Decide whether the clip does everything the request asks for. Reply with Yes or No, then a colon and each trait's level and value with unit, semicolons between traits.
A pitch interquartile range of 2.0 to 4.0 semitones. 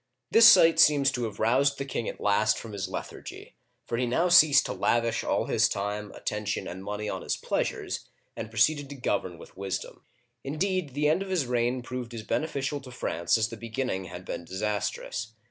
No: average, 5.2 semitones